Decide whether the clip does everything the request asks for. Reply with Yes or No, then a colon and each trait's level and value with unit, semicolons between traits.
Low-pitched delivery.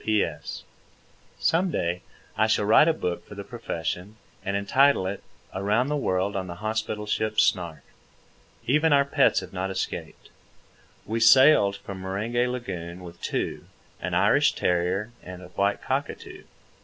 Yes: low, 100 Hz